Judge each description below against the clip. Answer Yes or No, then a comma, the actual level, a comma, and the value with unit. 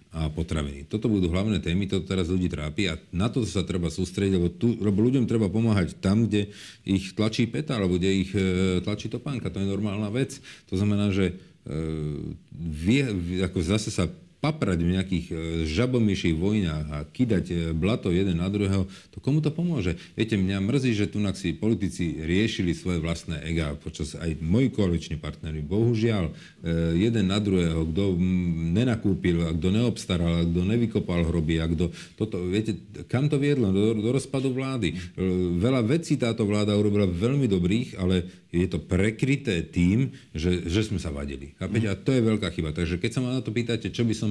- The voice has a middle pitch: No, very low, 95 Hz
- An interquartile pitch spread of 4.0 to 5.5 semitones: Yes, average, 4.4 semitones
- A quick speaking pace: Yes, fast, 175 wpm